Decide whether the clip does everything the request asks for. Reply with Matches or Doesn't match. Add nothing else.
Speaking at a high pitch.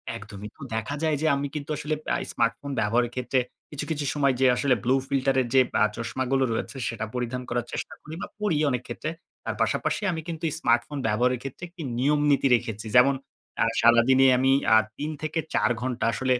Doesn't match